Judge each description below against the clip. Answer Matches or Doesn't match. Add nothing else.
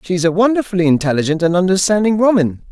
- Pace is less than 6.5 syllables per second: Doesn't match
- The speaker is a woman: Doesn't match